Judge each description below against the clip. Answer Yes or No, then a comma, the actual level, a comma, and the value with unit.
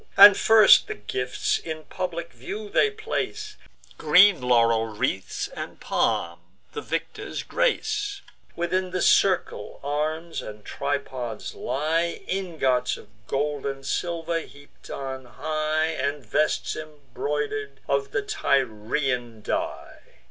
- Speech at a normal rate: No, slow, 115 wpm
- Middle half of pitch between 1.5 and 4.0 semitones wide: No, average, 5.3 semitones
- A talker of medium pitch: Yes, medium, 150 Hz